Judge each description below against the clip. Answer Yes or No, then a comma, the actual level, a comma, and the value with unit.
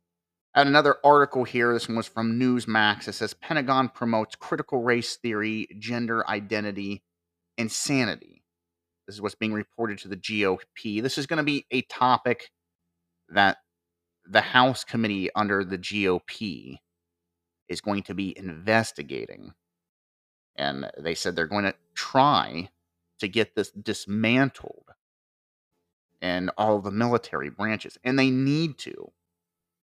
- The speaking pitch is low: Yes, low, 105 Hz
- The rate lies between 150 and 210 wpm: No, slow, 135 wpm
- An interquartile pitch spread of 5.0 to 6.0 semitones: Yes, average, 5.3 semitones